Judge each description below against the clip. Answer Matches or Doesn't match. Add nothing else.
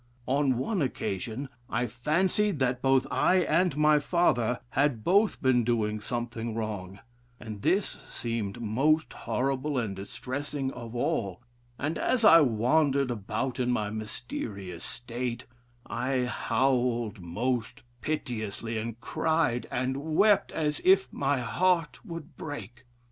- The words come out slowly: Matches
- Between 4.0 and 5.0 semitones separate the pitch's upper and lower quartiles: Matches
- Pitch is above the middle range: Doesn't match